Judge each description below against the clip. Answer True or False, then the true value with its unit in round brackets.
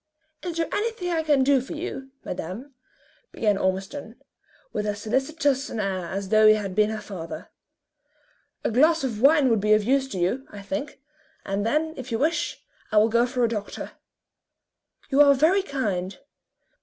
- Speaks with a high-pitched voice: True (245 Hz)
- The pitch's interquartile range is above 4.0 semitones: True (5.6 semitones)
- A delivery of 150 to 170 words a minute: False (180 wpm)